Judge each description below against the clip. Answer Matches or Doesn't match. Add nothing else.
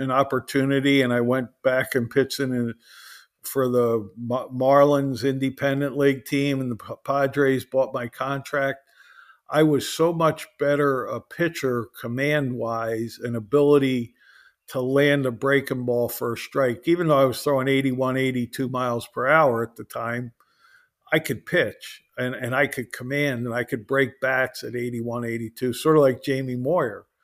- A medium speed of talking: Matches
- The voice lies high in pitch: Doesn't match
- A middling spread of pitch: Doesn't match